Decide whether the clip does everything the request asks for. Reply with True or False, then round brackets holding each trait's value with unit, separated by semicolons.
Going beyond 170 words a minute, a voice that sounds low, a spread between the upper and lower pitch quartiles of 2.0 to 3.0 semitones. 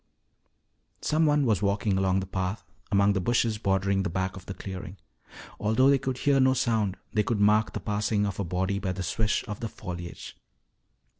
True (190 wpm; 100 Hz; 2.7 semitones)